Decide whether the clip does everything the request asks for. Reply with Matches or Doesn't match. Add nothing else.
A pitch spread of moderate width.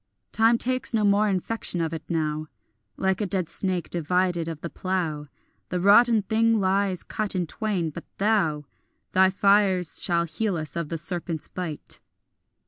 Matches